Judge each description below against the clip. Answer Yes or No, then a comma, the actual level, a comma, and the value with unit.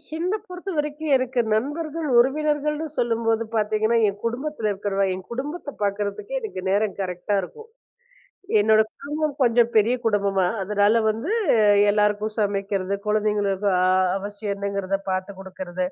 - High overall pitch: Yes, high, 215 Hz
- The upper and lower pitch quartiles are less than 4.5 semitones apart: No, average, 5.2 semitones